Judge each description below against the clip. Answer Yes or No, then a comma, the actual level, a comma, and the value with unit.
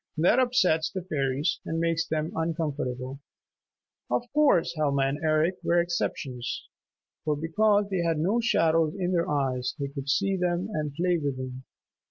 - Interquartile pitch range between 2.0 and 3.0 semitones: No, average, 4.0 semitones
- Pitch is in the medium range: Yes, medium, 160 Hz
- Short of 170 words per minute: Yes, average, 160 wpm